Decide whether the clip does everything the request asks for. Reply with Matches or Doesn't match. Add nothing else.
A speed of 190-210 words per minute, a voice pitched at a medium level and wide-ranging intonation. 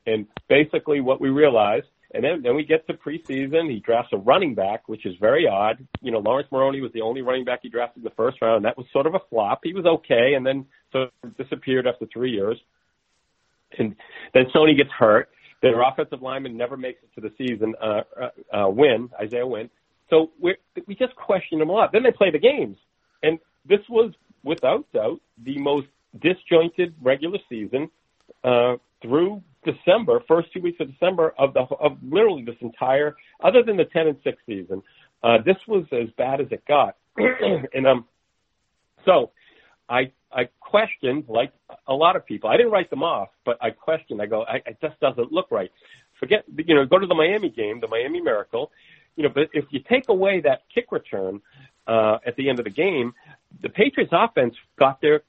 Matches